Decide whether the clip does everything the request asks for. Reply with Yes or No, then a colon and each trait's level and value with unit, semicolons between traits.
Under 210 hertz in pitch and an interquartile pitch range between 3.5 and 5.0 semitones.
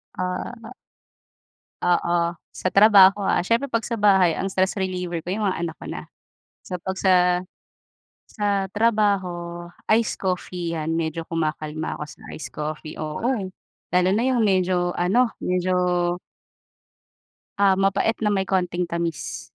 No: medium, 185 Hz; average, 2.8 semitones